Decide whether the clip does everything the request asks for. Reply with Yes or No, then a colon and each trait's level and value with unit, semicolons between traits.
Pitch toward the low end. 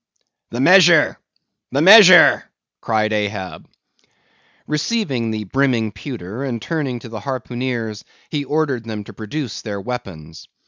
Yes: low, 120 Hz